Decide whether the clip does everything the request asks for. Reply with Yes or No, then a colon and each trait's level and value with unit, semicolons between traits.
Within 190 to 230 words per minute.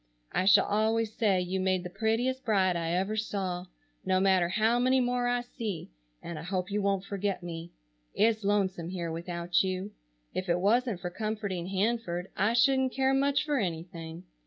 No: average, 180 wpm